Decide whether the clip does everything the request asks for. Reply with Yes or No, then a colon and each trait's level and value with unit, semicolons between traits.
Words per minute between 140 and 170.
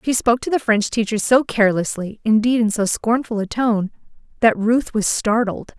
Yes: average, 165 wpm